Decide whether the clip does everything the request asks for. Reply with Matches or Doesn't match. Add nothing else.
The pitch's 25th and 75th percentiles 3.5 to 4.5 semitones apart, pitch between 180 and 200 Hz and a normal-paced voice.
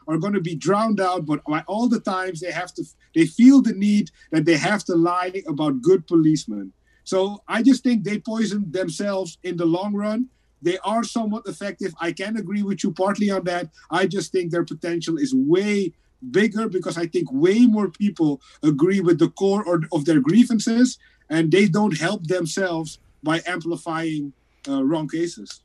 Matches